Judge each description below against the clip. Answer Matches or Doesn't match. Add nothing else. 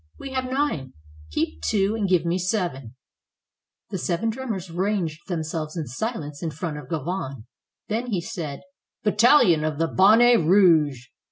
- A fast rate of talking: Doesn't match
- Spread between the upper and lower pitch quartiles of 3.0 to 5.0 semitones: Doesn't match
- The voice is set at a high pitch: Doesn't match